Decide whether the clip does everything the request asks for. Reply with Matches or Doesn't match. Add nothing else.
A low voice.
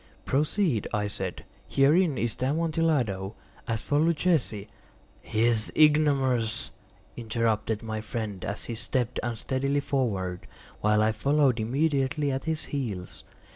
Matches